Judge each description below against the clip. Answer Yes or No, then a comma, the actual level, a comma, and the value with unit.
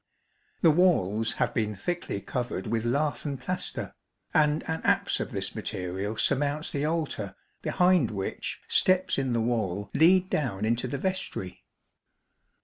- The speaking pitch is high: No, low, 130 Hz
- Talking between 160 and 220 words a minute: No, average, 140 wpm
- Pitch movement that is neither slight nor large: No, wide, 7.0 semitones